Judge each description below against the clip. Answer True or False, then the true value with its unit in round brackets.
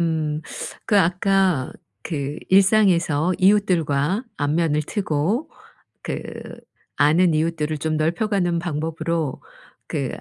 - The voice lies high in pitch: False (165 Hz)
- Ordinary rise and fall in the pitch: True (3.7 semitones)